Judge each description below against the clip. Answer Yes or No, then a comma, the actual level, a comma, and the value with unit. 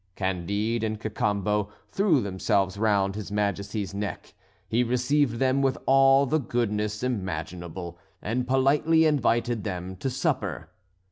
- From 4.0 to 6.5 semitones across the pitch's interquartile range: Yes, average, 4.5 semitones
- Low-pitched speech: Yes, low, 110 Hz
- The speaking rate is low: Yes, slow, 125 wpm